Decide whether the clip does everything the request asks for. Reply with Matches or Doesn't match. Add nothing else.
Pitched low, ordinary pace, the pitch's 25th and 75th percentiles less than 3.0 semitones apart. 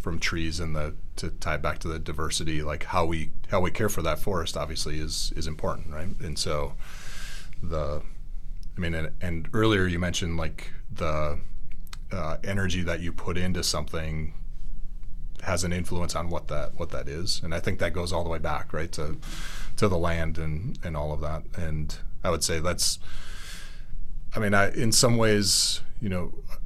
Matches